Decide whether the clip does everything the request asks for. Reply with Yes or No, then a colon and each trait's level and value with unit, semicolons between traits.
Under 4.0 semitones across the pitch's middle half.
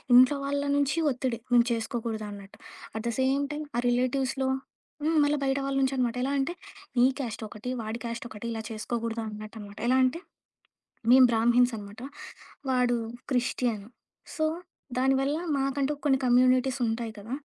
Yes: average, 2.9 semitones